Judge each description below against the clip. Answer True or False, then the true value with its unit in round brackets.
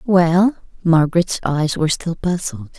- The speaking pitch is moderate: True (170 Hz)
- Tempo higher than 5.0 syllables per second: False (4.3 syllables/s)